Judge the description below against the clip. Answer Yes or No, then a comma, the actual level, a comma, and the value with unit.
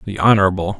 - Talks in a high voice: No, very low, 95 Hz